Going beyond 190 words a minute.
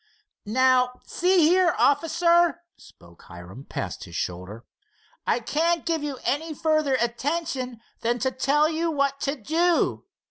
No: slow, 135 wpm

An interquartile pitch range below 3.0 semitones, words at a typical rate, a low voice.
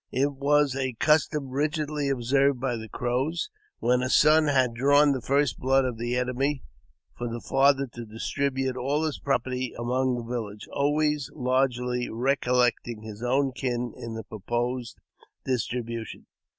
Yes: narrow, 2.6 semitones; average, 155 wpm; low, 130 Hz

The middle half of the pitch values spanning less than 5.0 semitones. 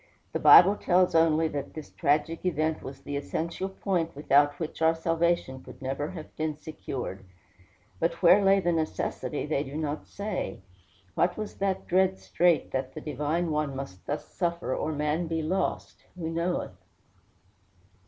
Yes: average, 3.1 semitones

